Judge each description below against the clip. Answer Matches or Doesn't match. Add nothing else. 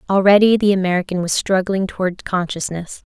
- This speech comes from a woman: Matches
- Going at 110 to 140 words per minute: Matches